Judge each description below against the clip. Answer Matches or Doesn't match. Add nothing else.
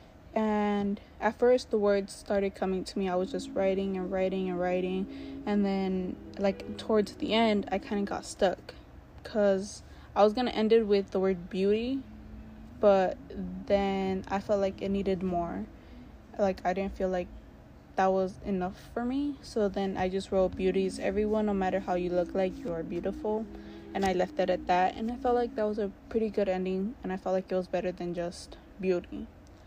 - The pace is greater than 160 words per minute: Matches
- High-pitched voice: Matches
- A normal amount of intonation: Doesn't match